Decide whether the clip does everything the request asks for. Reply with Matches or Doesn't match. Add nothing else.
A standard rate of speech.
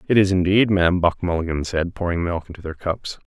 Doesn't match